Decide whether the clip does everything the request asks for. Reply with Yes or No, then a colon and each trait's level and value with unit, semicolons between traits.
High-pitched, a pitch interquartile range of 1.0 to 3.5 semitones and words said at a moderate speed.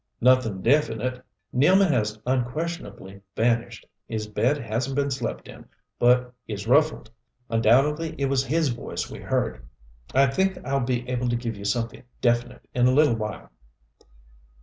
No: low, 125 Hz; average, 3.2 semitones; average, 150 wpm